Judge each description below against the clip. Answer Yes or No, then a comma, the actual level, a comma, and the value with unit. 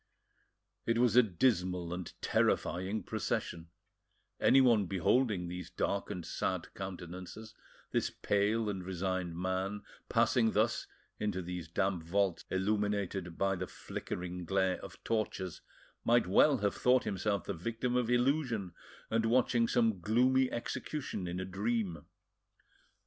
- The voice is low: Yes, low, 100 Hz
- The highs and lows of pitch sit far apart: No, average, 4.1 semitones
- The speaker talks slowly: Yes, slow, 125 wpm